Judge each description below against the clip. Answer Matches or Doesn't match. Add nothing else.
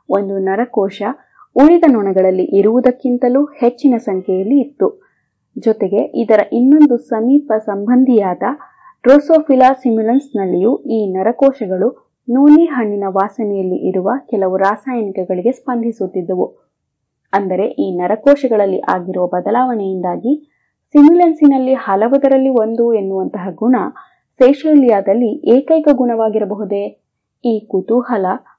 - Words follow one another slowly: Matches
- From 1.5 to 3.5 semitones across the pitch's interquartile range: Doesn't match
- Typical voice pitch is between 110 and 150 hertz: Doesn't match